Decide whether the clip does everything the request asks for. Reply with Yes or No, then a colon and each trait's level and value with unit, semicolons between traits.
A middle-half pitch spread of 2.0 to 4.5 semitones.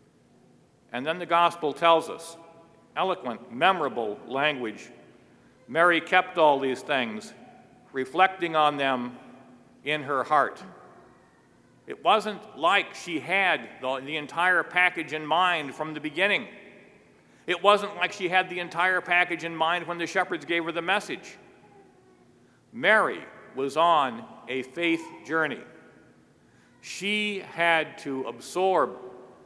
Yes: average, 3.7 semitones